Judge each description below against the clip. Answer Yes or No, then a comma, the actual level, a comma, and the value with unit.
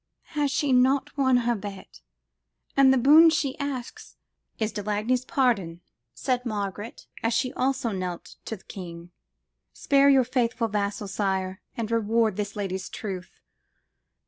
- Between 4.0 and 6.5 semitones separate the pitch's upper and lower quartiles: Yes, average, 4.7 semitones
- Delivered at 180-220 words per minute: No, average, 145 wpm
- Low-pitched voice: No, high, 230 Hz